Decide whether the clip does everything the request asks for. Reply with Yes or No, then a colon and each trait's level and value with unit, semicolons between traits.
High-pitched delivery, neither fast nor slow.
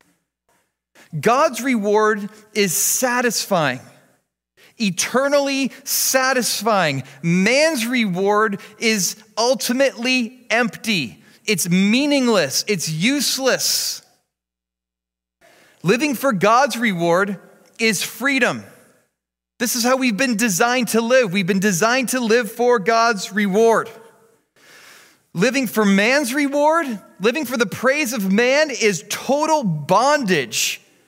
No: high, 225 Hz; slow, 95 wpm